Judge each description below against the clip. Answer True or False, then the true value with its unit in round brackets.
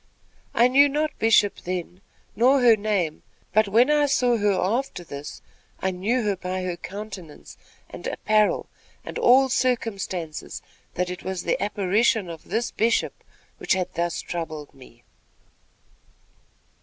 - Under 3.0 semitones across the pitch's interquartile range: False (4.7 semitones)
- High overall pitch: True (200 Hz)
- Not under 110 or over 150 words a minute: True (140 wpm)